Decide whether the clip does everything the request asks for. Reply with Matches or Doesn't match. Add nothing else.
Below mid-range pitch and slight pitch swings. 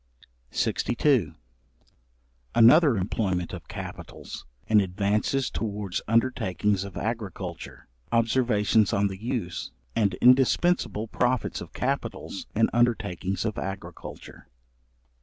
Doesn't match